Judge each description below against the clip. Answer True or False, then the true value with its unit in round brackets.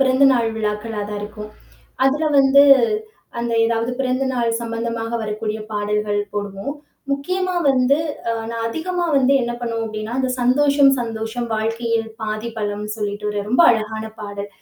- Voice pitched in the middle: False (230 Hz)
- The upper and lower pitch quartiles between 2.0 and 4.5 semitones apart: True (3.3 semitones)